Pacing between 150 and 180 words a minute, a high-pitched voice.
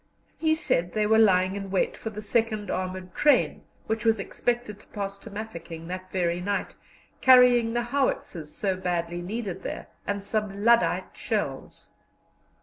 Yes: average, 155 wpm; high, 205 Hz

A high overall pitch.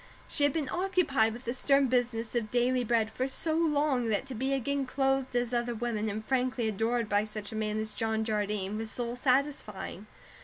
Yes: high, 240 Hz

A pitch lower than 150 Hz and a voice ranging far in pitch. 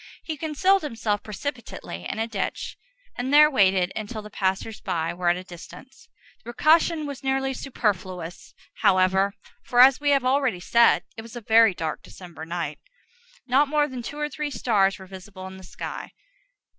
No: high, 225 Hz; wide, 6.4 semitones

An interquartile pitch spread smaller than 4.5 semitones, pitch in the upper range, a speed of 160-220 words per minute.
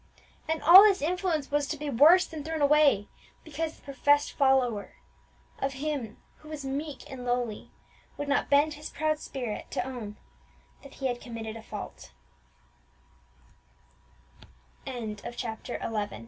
No: average, 4.1 semitones; very high, 280 Hz; average, 140 wpm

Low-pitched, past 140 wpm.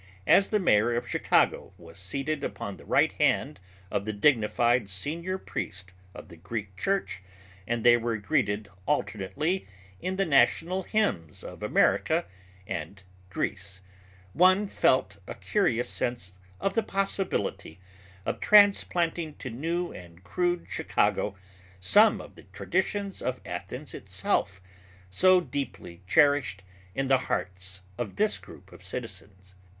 No: low, 120 Hz; slow, 135 wpm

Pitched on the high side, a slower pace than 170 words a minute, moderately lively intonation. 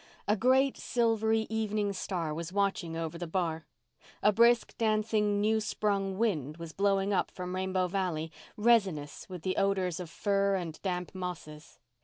Yes: high, 195 Hz; average, 155 wpm; average, 3.6 semitones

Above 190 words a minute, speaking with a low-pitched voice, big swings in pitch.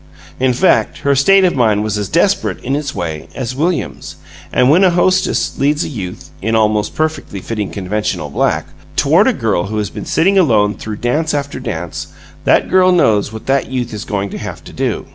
Yes: average, 200 wpm; low, 125 Hz; wide, 7.1 semitones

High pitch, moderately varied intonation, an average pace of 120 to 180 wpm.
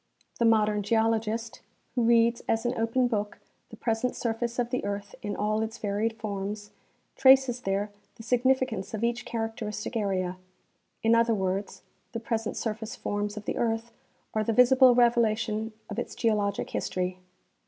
No: high, 225 Hz; narrow, 2.1 semitones; average, 160 wpm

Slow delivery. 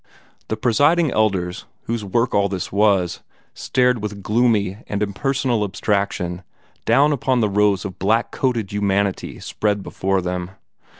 Yes: slow, 130 wpm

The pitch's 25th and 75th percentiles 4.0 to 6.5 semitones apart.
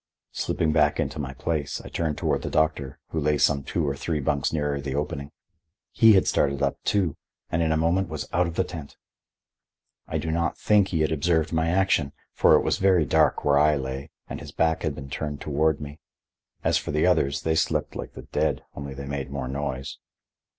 No: average, 2.7 semitones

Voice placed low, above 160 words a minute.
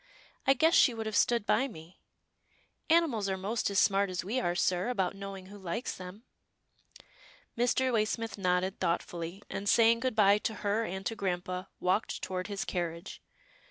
No: high, 200 Hz; average, 175 wpm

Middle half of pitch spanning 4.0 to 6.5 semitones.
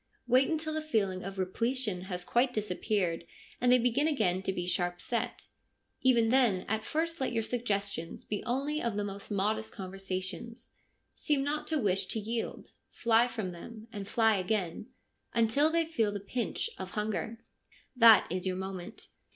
Yes: average, 4.5 semitones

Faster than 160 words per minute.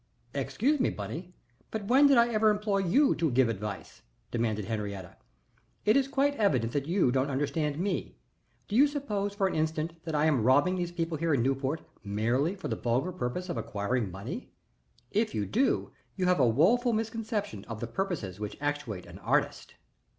Yes: average, 185 wpm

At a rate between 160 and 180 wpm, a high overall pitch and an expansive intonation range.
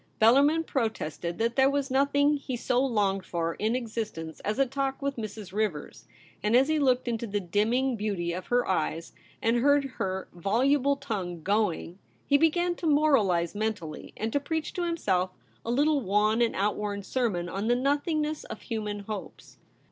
Yes: average, 175 wpm; high, 225 Hz; wide, 5.8 semitones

